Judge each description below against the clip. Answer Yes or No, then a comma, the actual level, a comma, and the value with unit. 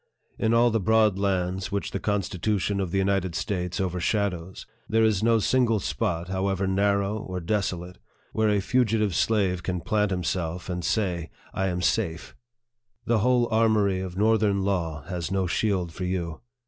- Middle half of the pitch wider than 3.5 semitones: No, average, 3.0 semitones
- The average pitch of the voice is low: Yes, very low, 95 Hz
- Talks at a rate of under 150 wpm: No, average, 175 wpm